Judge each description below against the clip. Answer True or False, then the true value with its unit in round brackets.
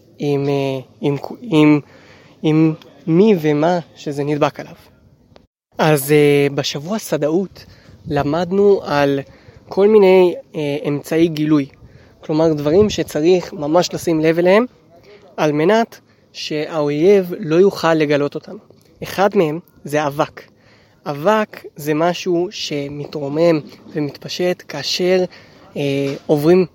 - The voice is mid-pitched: True (155 Hz)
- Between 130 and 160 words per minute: False (100 wpm)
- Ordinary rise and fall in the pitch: True (3.7 semitones)